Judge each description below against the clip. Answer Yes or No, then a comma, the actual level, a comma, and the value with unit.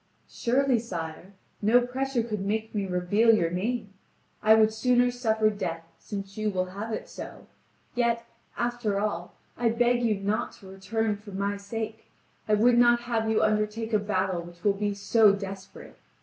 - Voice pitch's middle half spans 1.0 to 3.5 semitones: Yes, average, 2.8 semitones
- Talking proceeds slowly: No, average, 170 wpm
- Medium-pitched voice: No, high, 215 Hz